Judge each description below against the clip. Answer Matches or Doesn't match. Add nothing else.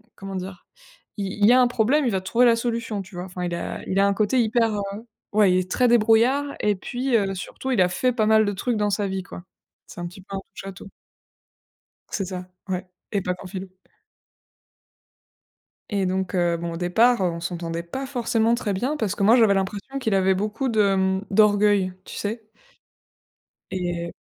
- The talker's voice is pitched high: Matches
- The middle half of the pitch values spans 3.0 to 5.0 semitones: Matches